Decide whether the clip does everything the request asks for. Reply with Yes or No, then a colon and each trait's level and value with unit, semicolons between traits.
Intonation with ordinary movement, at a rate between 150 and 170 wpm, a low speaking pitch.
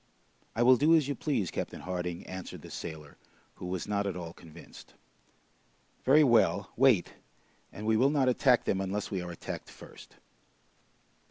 No: wide, 6.3 semitones; average, 165 wpm; low, 100 Hz